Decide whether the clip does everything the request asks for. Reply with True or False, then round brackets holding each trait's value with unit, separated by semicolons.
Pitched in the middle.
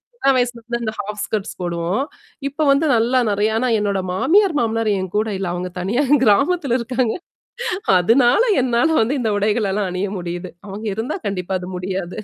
False (220 Hz)